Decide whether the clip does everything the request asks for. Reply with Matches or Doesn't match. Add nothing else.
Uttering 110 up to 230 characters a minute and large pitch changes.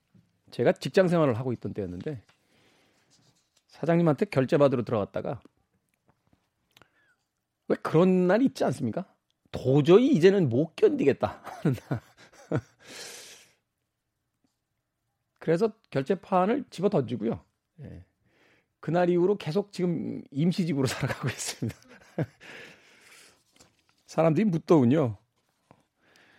Matches